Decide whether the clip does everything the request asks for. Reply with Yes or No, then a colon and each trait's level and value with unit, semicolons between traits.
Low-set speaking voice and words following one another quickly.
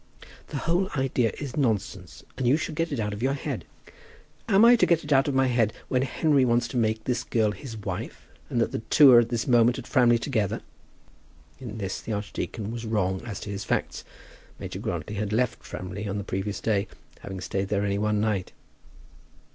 Yes: low, 115 Hz; fast, 210 wpm